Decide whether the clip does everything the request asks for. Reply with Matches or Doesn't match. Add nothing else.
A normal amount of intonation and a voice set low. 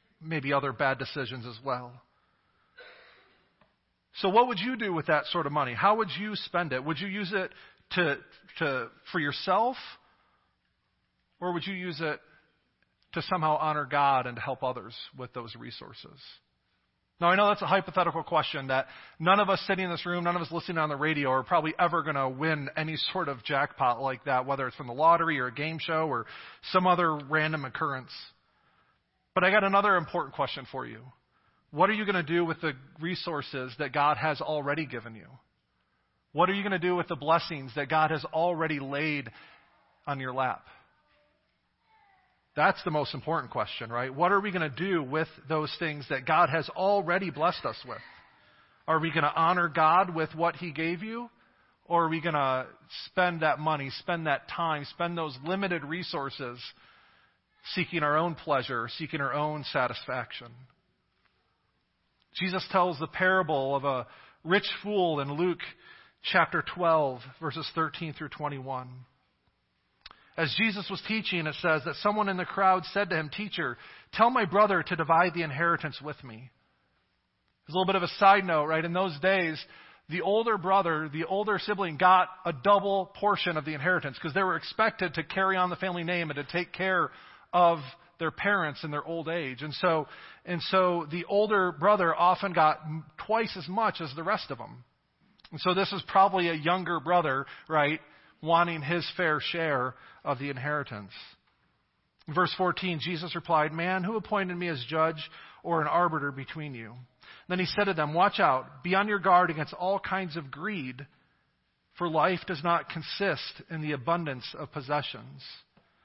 Doesn't match